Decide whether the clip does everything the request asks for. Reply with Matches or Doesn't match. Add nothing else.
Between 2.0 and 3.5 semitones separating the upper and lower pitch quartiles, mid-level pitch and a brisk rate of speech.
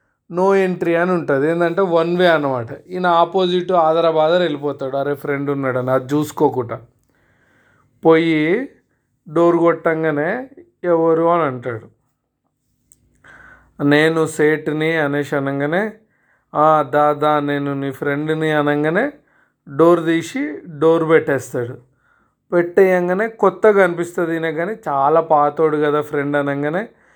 Doesn't match